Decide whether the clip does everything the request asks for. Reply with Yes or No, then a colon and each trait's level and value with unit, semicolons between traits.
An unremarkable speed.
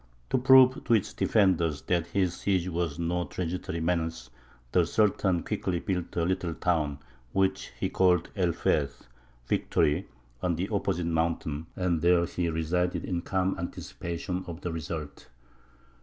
Yes: average, 145 wpm